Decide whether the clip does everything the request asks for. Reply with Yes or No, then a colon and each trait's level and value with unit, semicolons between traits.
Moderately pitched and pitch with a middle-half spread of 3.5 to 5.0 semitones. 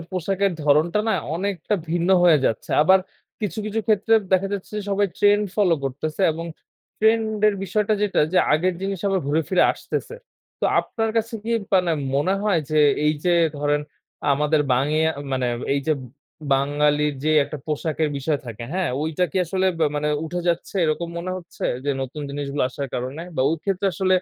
Yes: medium, 170 Hz; average, 4.6 semitones